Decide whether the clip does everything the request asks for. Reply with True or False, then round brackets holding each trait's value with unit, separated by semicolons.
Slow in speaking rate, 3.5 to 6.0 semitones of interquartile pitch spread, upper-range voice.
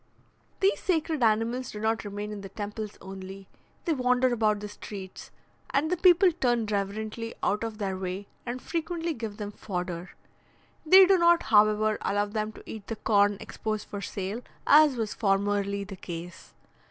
False (165 wpm; 3.8 semitones; 215 Hz)